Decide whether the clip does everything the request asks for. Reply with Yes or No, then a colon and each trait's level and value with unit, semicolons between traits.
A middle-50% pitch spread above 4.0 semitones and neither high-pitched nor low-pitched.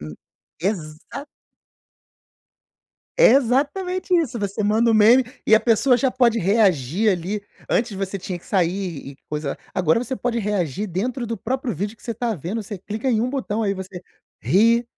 No: average, 4.4 semitones; high, 215 Hz